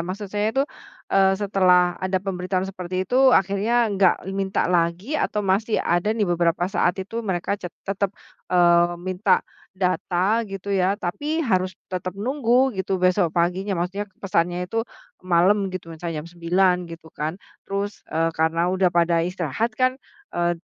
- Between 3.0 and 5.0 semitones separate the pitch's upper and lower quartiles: No, narrow, 2.4 semitones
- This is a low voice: No, medium, 185 Hz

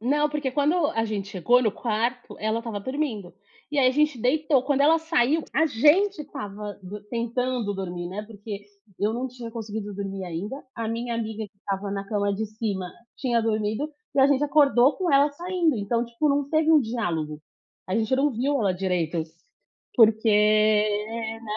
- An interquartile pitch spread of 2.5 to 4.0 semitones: No, average, 5.0 semitones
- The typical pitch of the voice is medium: No, high, 230 Hz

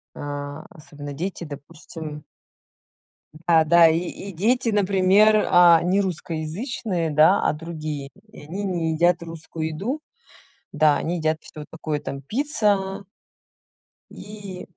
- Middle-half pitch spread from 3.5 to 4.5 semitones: Yes, average, 4.0 semitones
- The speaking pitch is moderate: Yes, medium, 170 Hz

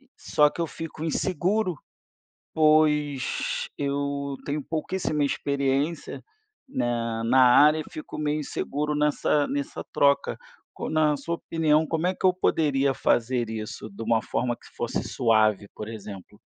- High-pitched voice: No, medium, 145 Hz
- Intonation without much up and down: No, average, 4.2 semitones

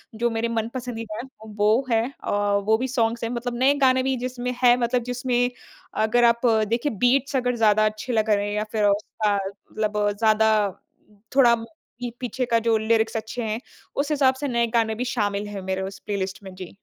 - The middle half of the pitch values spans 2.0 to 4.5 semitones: Yes, narrow, 2.6 semitones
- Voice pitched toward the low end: No, high, 230 Hz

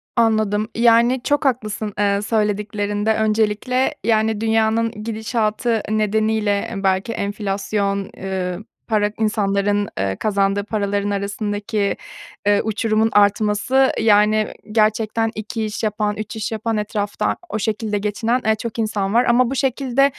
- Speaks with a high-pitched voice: Yes, high, 215 Hz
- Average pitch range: No, narrow, 1.6 semitones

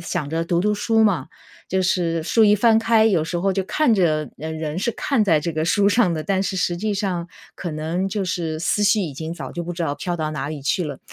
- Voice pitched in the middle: Yes, medium, 175 Hz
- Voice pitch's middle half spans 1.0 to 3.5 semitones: No, average, 4.3 semitones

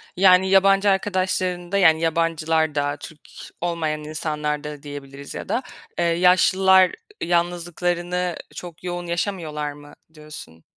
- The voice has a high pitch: No, medium, 170 Hz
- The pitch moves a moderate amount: Yes, average, 3.1 semitones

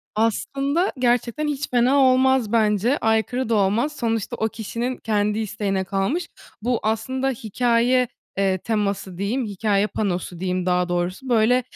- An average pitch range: Yes, average, 4.0 semitones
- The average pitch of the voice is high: Yes, high, 225 Hz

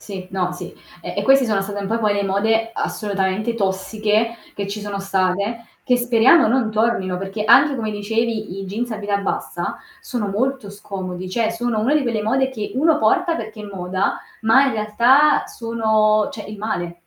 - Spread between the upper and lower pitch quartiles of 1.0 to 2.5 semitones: No, average, 2.9 semitones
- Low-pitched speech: No, high, 215 Hz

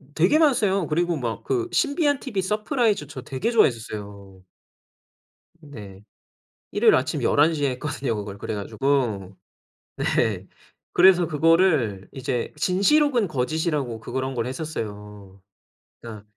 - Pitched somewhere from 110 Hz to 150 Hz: Yes, medium, 140 Hz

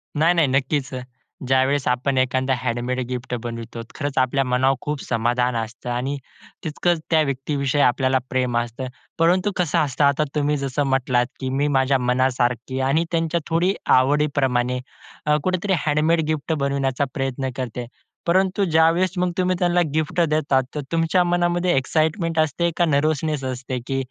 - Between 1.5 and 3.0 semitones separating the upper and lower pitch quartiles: No, average, 3.8 semitones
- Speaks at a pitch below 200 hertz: Yes, medium, 140 Hz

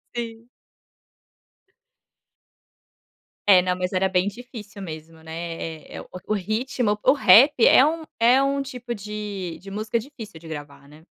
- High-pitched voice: Yes, high, 210 Hz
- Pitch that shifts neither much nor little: No, wide, 5.7 semitones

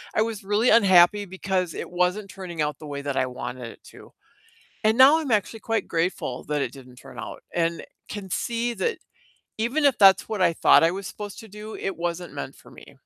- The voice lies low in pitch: No, high, 190 Hz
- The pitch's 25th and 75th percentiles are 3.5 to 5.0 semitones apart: Yes, average, 4.6 semitones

